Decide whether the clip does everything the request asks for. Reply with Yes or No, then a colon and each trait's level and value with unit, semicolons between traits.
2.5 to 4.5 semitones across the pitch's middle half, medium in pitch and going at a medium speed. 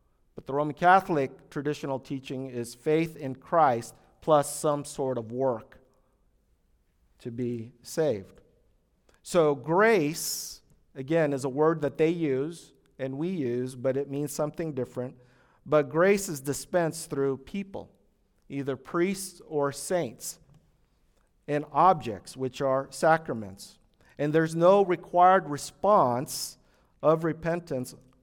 No: average, 3.8 semitones; medium, 145 Hz; slow, 120 wpm